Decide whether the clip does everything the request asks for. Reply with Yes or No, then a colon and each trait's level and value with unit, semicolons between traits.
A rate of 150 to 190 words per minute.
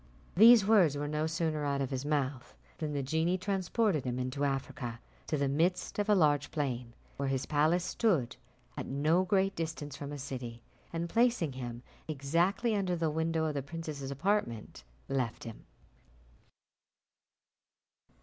Yes: average, 155 wpm